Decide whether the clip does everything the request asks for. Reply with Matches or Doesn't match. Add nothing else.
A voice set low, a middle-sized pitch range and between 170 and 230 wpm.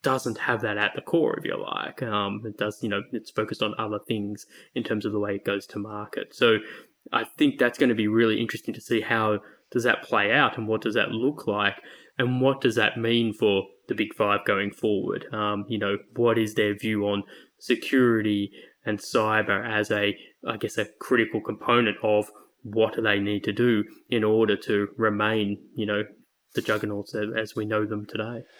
Doesn't match